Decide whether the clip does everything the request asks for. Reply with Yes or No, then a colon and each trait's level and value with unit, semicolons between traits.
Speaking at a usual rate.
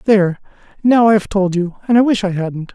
No: fast, 220 wpm